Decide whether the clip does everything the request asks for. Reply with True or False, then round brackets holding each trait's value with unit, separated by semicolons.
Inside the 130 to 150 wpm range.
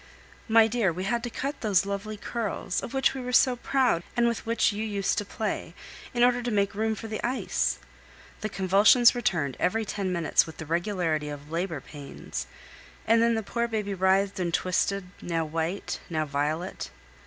False (190 wpm)